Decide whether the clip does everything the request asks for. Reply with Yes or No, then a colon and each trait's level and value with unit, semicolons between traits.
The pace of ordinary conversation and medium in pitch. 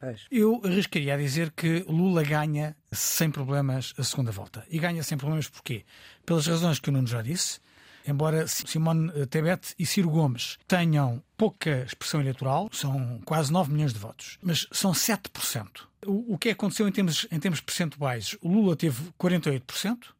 Yes: average, 165 wpm; medium, 160 Hz